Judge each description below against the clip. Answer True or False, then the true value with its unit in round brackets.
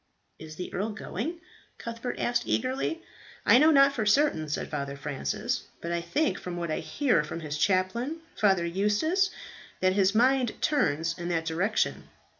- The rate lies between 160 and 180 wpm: True (165 wpm)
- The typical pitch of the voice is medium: False (200 Hz)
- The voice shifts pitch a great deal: True (7.8 semitones)